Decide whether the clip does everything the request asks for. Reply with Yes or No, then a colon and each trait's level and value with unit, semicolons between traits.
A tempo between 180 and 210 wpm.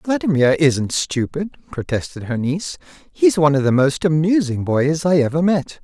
No: average, 165 wpm